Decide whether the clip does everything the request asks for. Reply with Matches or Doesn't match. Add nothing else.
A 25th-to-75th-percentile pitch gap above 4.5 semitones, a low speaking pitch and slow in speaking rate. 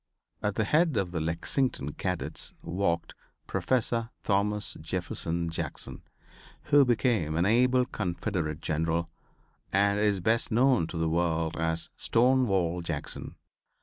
Matches